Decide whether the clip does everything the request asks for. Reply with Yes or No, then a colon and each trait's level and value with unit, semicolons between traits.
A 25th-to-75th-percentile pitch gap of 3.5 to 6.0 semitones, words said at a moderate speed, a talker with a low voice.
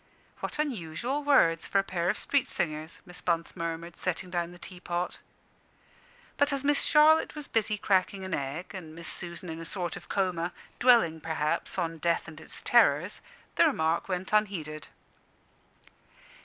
No: average, 3.9 semitones; average, 165 wpm; medium, 175 Hz